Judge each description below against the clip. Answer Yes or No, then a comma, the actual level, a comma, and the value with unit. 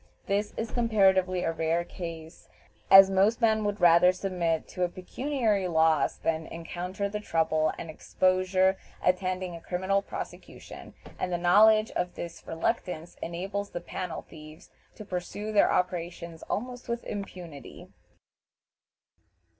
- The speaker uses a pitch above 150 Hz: Yes, medium, 185 Hz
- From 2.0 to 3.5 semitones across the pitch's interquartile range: Yes, average, 3.1 semitones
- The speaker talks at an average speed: No, slow, 130 wpm